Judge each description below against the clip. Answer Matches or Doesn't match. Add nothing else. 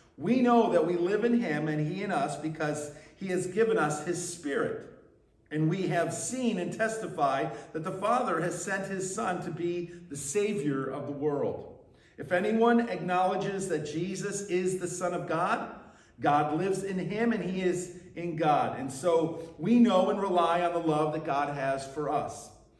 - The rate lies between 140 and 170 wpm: Doesn't match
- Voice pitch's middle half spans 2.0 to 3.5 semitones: Doesn't match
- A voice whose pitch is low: Doesn't match